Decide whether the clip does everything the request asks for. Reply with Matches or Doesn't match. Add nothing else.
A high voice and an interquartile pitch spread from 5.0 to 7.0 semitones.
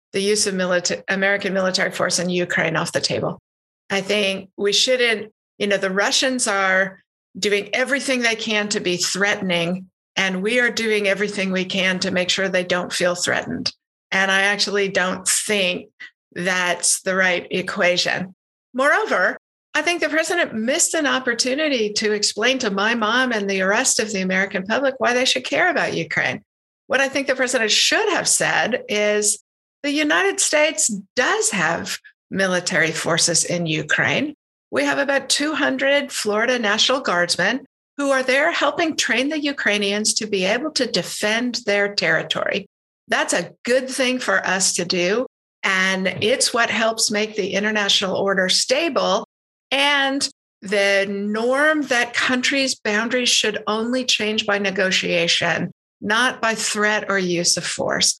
Matches